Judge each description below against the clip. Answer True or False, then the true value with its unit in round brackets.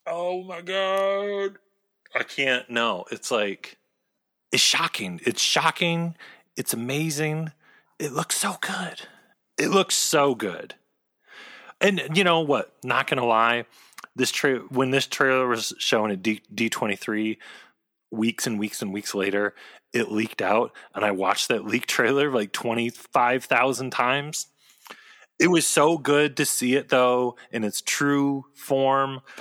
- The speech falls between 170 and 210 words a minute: False (145 wpm)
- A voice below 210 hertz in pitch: True (135 Hz)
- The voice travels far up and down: True (6.1 semitones)